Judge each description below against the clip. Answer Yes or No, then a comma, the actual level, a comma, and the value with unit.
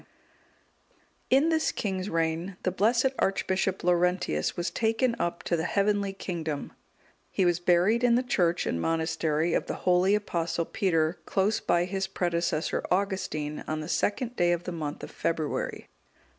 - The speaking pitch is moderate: Yes, medium, 180 Hz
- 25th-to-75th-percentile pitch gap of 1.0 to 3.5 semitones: Yes, average, 3.2 semitones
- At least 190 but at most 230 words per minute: No, average, 155 wpm